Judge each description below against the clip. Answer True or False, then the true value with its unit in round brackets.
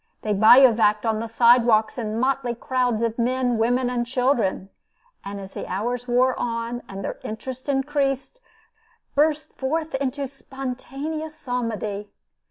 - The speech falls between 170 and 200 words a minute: False (140 wpm)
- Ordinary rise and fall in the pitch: True (3.2 semitones)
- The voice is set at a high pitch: True (245 Hz)